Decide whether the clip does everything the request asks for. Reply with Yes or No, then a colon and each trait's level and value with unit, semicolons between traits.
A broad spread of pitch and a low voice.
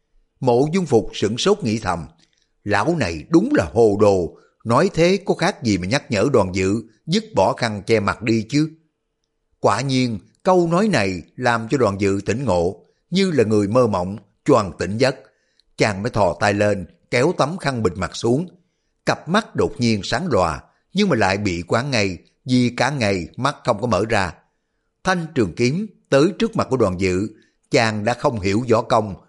Yes: wide, 7.0 semitones; low, 120 Hz